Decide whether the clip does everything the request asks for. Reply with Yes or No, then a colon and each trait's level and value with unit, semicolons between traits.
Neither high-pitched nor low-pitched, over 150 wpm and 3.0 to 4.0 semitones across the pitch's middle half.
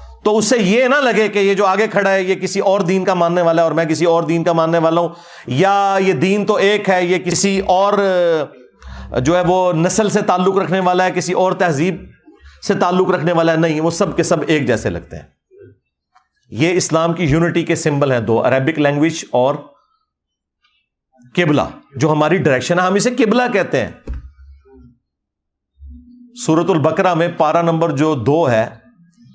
Yes: medium, 175 Hz; fast, 190 wpm; average, 3.7 semitones